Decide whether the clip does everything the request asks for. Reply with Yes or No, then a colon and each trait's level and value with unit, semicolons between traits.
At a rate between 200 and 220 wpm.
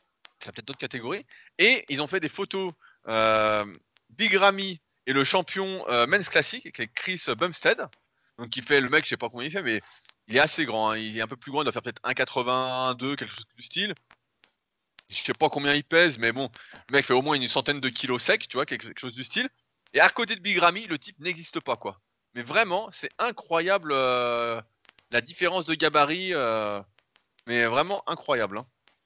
Yes: average, 215 wpm